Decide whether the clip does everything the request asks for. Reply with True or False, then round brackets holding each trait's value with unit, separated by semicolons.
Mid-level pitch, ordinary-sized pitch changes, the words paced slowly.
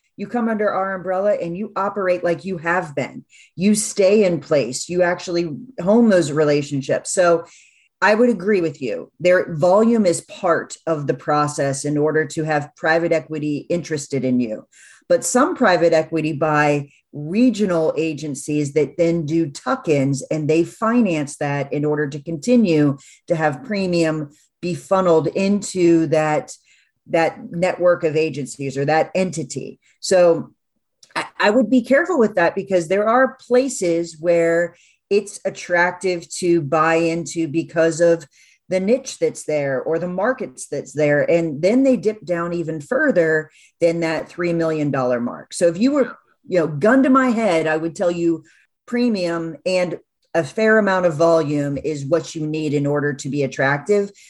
False (170 Hz; 3.7 semitones; 165 wpm)